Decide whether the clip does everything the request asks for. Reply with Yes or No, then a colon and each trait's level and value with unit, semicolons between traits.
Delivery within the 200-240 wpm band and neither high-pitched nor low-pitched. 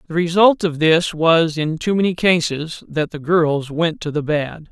Yes: fast, 205 wpm; medium, 160 Hz